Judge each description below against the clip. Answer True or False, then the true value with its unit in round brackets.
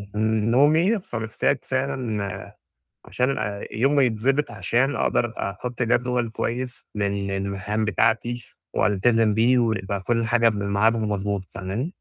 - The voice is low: True (115 Hz)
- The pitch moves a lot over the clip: False (3.3 semitones)